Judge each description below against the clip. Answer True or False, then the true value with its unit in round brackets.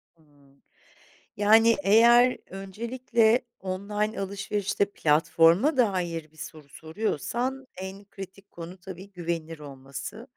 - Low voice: False (195 Hz)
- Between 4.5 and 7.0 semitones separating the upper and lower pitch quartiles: True (4.9 semitones)